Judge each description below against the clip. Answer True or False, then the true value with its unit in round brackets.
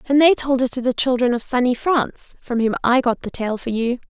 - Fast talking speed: True (265 wpm)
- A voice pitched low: False (250 Hz)